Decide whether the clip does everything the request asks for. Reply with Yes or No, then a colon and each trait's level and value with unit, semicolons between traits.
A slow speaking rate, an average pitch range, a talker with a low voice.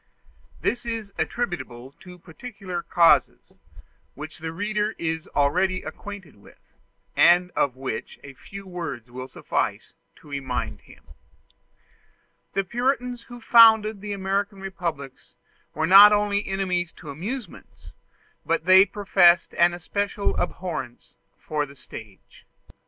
No: slow, 120 wpm; average, 4.6 semitones; medium, 180 Hz